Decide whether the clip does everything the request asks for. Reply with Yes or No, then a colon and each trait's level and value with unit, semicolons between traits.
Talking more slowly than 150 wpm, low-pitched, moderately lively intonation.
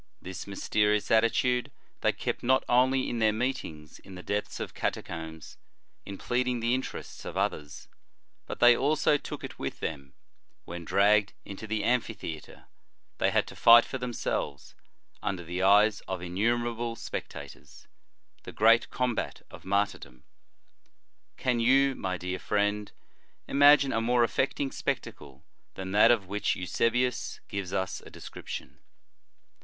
Yes: average, 140 wpm; low, 105 Hz; average, 4.5 semitones